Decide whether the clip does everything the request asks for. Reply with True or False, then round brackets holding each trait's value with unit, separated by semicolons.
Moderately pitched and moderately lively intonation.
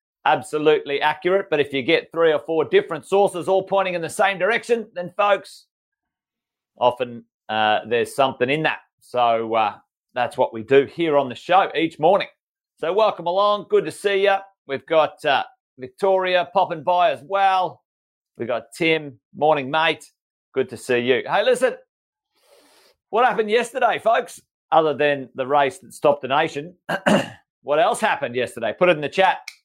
False (175 Hz; 5.7 semitones)